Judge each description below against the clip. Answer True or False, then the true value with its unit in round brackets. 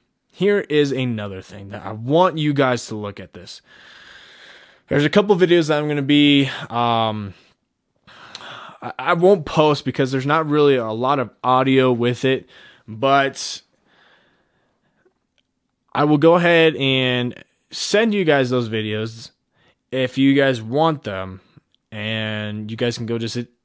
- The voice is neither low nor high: False (130 Hz)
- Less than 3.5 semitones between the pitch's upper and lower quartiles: False (4.7 semitones)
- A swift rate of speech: False (150 wpm)